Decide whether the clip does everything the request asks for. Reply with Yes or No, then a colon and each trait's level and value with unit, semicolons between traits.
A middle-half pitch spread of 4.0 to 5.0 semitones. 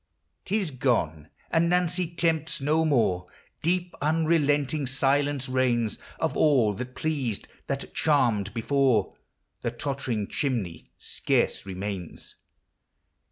No: wide, 5.4 semitones